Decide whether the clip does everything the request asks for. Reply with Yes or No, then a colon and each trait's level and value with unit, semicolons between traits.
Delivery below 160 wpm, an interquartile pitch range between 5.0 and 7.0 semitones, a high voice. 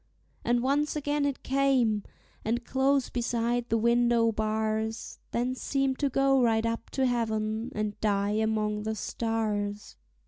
No: average, 140 wpm; average, 3.1 semitones; high, 230 Hz